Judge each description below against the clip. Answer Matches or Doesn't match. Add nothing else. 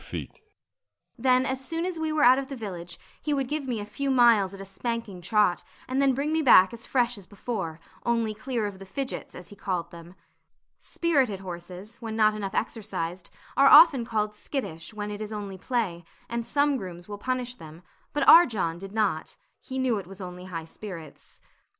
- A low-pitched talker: Doesn't match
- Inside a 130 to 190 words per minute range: Doesn't match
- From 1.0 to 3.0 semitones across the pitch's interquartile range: Doesn't match